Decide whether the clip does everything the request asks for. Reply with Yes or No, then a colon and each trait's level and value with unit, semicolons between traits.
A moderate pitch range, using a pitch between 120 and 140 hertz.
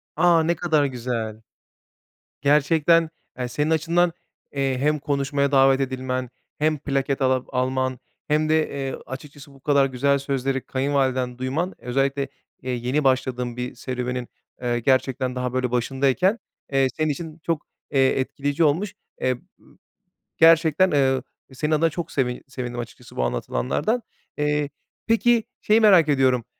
Yes: average, 3.0 semitones; low, 135 Hz